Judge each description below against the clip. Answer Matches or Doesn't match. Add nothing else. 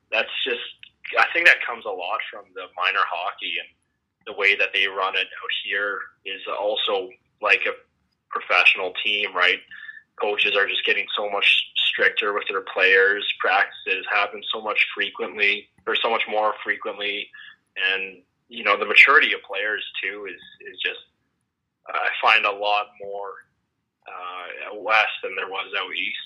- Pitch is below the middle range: Matches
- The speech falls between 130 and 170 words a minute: Matches